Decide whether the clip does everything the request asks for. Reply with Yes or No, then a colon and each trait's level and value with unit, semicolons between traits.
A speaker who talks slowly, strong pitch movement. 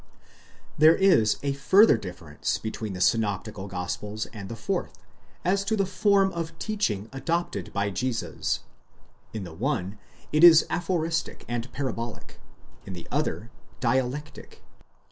Yes: slow, 130 wpm; wide, 8.3 semitones